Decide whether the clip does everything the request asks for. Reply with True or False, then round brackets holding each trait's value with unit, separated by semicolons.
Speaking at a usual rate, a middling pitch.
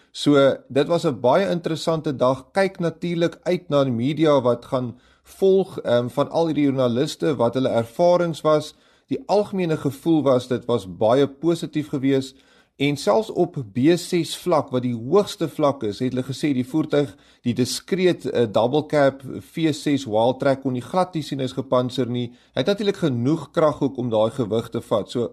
True (170 wpm; 145 Hz)